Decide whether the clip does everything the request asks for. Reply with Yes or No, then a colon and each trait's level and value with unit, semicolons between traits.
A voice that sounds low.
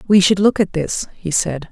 No: medium, 185 Hz